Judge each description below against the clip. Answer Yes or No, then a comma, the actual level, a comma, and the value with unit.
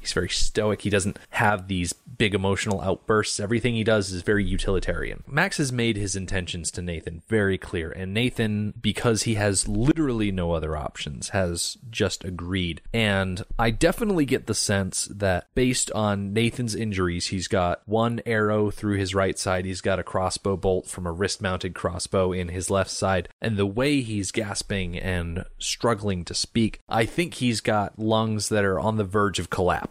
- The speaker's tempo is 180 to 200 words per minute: Yes, average, 185 wpm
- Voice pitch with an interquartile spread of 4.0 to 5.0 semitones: No, average, 3.1 semitones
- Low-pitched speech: Yes, low, 100 Hz